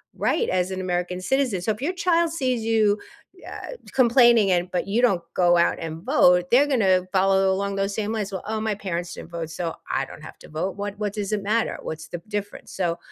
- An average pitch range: Yes, average, 3.9 semitones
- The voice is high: Yes, high, 200 Hz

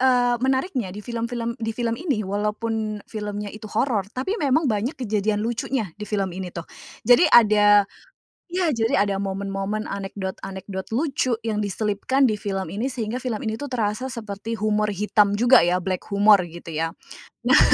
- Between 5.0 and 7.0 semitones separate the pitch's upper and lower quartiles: No, average, 3.1 semitones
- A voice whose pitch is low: No, high, 215 Hz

